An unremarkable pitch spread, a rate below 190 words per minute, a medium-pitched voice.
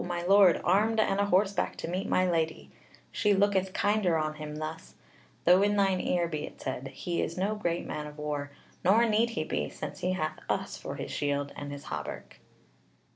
No: average, 4.6 semitones; average, 200 wpm; medium, 180 Hz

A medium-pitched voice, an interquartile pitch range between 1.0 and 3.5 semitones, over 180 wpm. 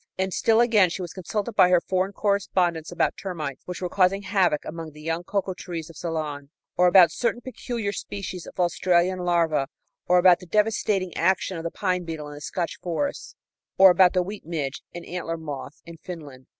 Yes: medium, 180 Hz; average, 2.7 semitones; average, 195 wpm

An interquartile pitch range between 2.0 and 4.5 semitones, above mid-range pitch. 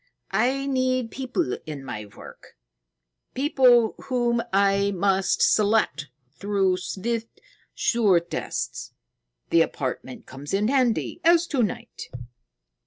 No: wide, 5.6 semitones; high, 210 Hz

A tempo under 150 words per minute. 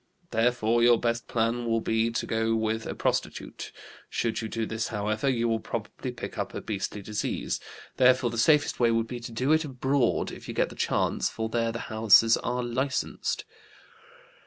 No: average, 185 wpm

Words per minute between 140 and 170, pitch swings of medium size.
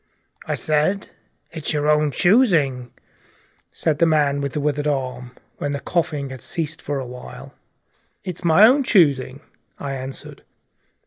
Yes: average, 145 wpm; average, 3.2 semitones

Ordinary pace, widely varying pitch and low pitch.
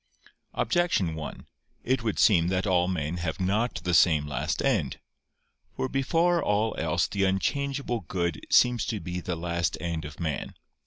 Yes: average, 160 wpm; wide, 6.0 semitones; very low, 90 Hz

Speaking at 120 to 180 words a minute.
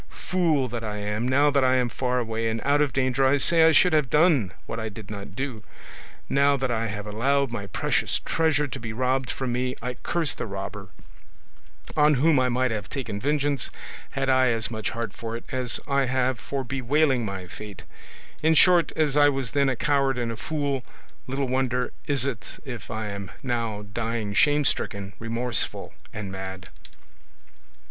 No: average, 190 wpm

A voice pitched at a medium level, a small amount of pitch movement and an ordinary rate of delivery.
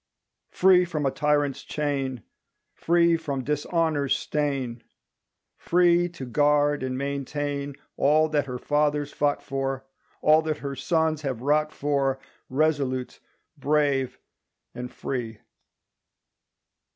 No: medium, 145 Hz; narrow, 2.2 semitones; slow, 110 wpm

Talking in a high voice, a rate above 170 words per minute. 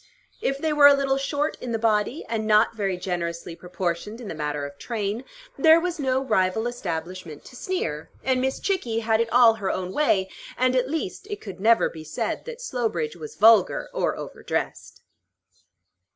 Yes: high, 225 Hz; average, 180 wpm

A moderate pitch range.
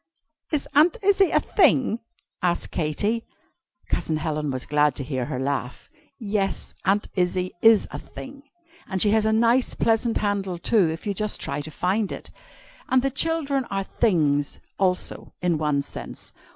No: wide, 6.9 semitones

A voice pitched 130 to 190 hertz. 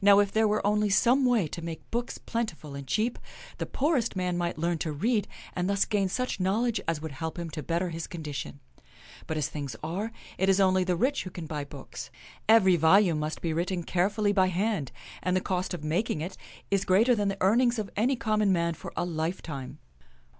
Yes: medium, 185 Hz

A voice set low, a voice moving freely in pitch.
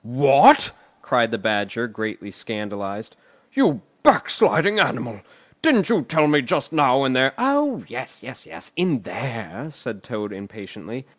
Yes: low, 120 Hz; wide, 6.1 semitones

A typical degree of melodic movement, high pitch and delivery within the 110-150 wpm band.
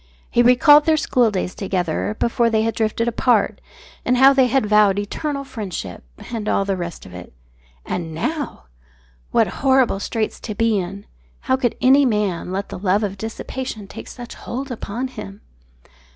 No: average, 4.4 semitones; high, 220 Hz; average, 165 wpm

